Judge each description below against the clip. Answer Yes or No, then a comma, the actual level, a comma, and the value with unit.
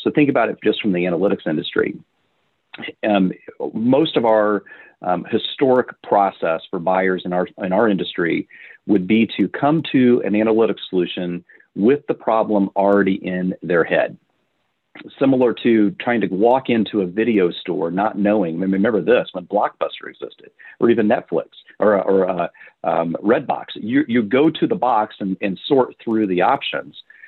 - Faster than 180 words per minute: No, average, 165 wpm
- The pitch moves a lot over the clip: Yes, wide, 5.9 semitones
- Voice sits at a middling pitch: No, low, 110 Hz